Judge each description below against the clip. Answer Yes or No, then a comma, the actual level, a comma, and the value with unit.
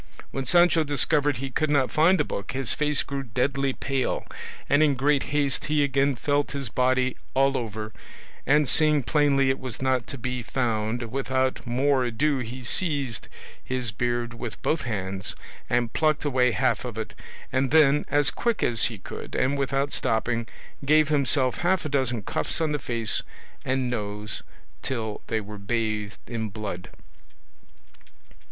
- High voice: No, low, 130 Hz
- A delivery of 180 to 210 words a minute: No, average, 160 wpm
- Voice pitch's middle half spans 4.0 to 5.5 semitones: No, average, 3.5 semitones